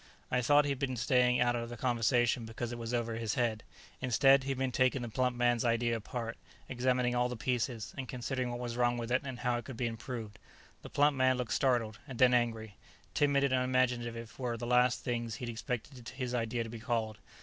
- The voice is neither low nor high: No, low, 120 Hz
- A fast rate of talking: Yes, fast, 220 wpm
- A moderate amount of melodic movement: No, narrow, 1.6 semitones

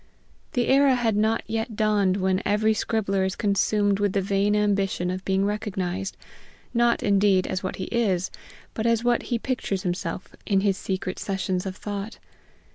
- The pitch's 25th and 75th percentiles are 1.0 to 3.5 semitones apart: Yes, narrow, 2.4 semitones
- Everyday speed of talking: Yes, average, 170 wpm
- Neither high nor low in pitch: No, high, 200 Hz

